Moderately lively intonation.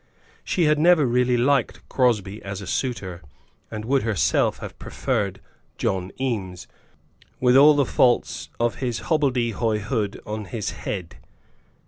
Yes: average, 4.5 semitones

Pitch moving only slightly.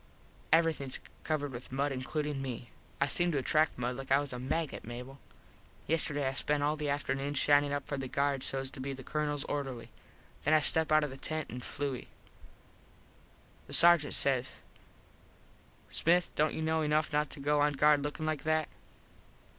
Yes: narrow, 2.2 semitones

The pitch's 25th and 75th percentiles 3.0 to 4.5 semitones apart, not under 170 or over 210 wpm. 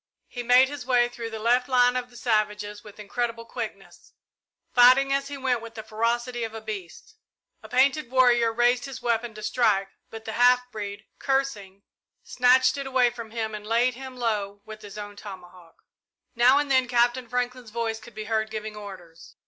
No: narrow, 2.6 semitones; average, 190 wpm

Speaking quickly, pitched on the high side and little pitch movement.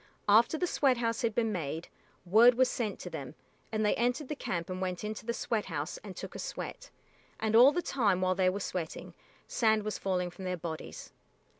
No: fast, 210 wpm; high, 210 Hz; average, 4.4 semitones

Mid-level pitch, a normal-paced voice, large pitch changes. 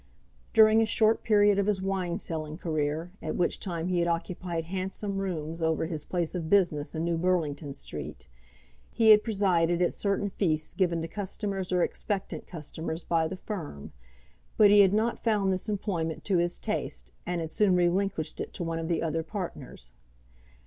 No: medium, 175 Hz; average, 180 wpm; average, 3.5 semitones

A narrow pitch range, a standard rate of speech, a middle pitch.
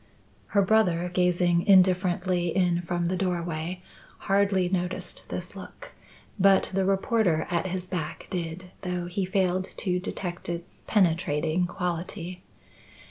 No: narrow, 1.4 semitones; slow, 125 wpm; medium, 180 Hz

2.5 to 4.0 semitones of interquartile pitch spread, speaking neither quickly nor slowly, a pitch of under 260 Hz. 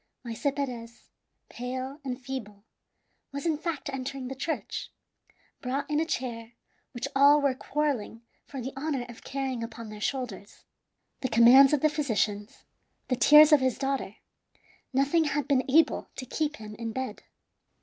No: average, 3.2 semitones; average, 155 wpm; very high, 265 Hz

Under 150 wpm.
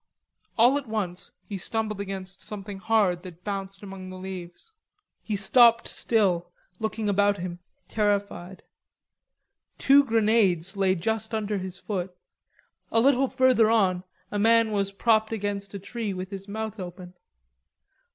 Yes: average, 140 wpm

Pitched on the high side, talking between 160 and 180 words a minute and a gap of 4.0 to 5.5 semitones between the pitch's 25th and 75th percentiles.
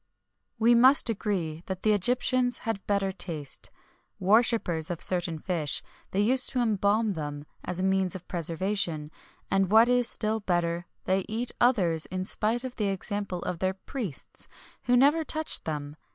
Yes: high, 195 Hz; average, 165 wpm; average, 4.9 semitones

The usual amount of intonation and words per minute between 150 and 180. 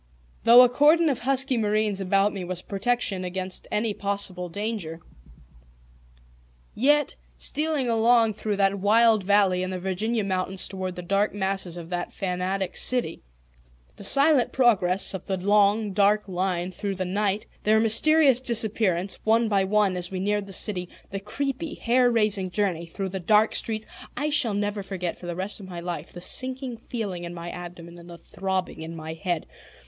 Yes: average, 3.6 semitones; average, 175 wpm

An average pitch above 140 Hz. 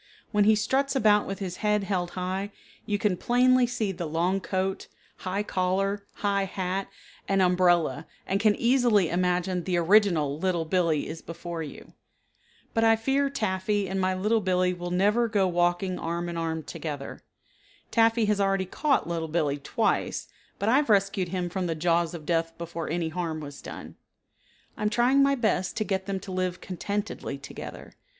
Yes: high, 190 Hz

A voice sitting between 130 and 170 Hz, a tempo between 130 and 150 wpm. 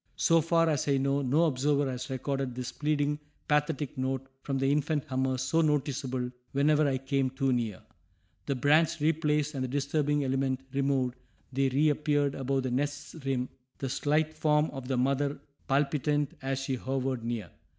No: medium, 140 Hz; average, 165 wpm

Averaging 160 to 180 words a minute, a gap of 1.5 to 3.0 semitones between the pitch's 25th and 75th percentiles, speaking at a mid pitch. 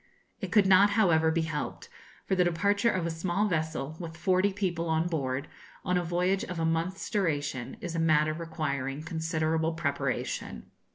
Yes: average, 170 wpm; narrow, 2.6 semitones; medium, 165 Hz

